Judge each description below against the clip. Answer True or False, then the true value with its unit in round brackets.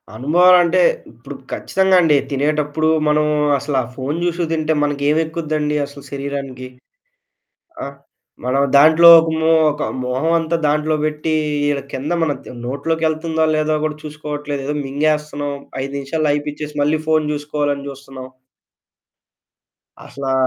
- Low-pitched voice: False (150 Hz)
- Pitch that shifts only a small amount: True (1.9 semitones)